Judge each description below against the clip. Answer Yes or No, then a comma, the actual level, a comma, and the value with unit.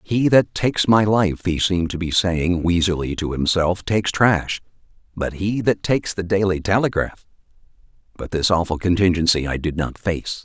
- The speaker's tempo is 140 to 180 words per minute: Yes, average, 170 wpm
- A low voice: Yes, very low, 90 Hz